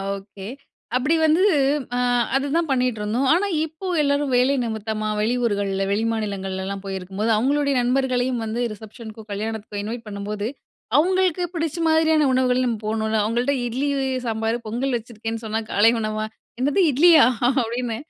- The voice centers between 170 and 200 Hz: No, high, 230 Hz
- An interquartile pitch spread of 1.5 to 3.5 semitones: No, average, 4.2 semitones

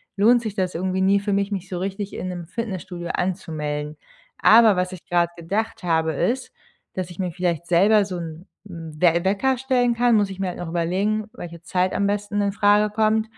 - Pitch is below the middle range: No, high, 190 Hz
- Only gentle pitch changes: No, average, 3.3 semitones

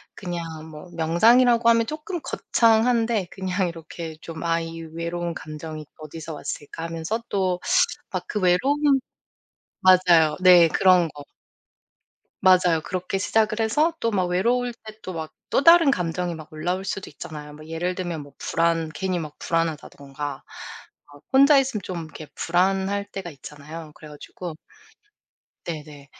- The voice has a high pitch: No, medium, 175 Hz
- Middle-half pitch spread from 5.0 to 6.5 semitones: No, average, 3.9 semitones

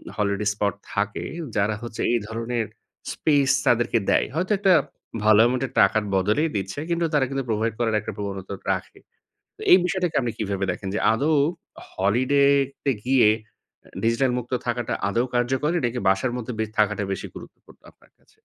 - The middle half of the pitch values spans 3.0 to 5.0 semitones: Yes, average, 4.1 semitones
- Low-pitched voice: Yes, low, 115 Hz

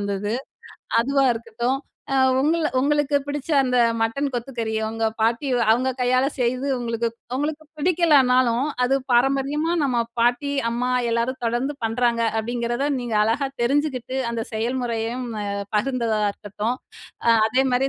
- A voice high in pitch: Yes, very high, 250 Hz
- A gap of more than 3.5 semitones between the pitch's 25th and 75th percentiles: No, average, 2.8 semitones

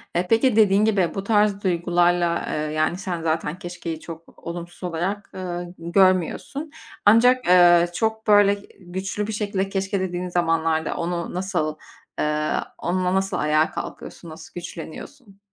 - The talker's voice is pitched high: No, medium, 180 Hz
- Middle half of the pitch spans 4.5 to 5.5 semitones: No, average, 2.8 semitones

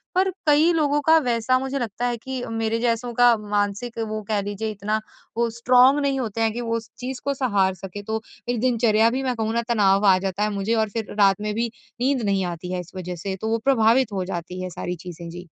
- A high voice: Yes, high, 225 Hz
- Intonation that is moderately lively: Yes, average, 3.7 semitones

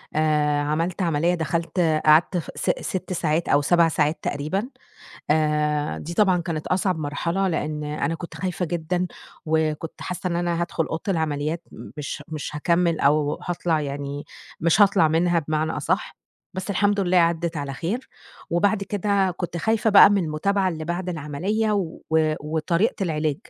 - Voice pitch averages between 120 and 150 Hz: No, medium, 165 Hz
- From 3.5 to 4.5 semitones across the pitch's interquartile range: No, average, 3.0 semitones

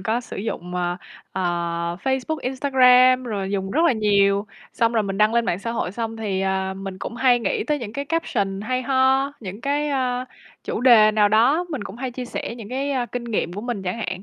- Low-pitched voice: No, high, 230 Hz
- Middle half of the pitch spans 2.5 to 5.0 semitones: Yes, average, 4.7 semitones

